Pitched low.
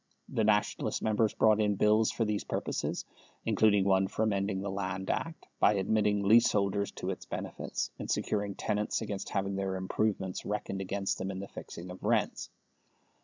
Yes: low, 100 Hz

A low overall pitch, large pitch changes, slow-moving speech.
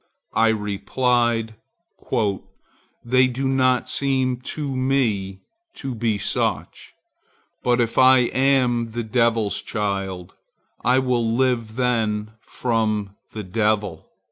No: low, 115 Hz; average, 3.0 semitones; slow, 105 wpm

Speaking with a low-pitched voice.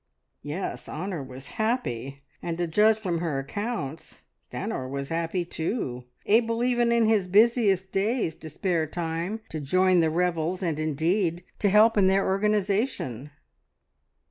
No: medium, 180 Hz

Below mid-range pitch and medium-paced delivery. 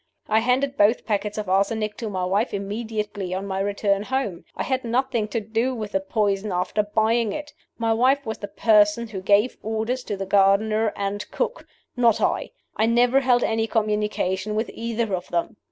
No: high, 215 Hz; average, 185 wpm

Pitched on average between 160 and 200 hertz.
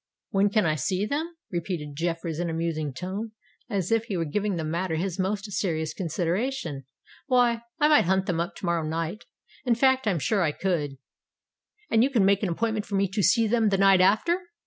Yes: high, 190 Hz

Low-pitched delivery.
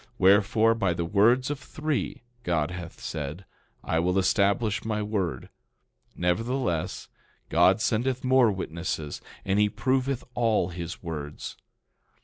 Yes: low, 100 Hz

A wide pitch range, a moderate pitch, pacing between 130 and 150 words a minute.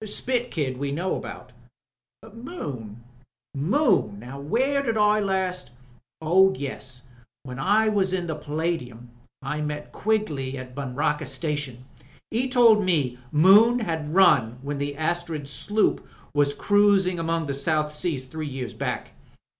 Yes: wide, 6.3 semitones; medium, 155 Hz; average, 140 wpm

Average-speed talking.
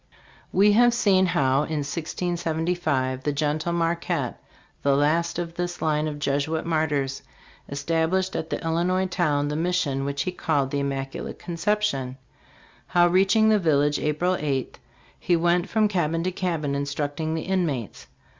Yes: average, 145 wpm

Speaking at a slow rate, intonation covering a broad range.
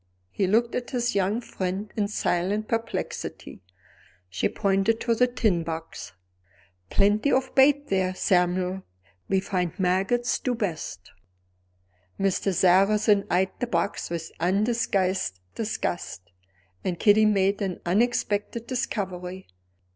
No: slow, 115 wpm; average, 3.5 semitones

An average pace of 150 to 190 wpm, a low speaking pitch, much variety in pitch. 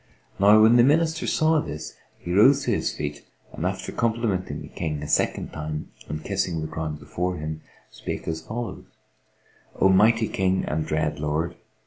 Yes: average, 170 wpm; very low, 90 Hz; wide, 6.5 semitones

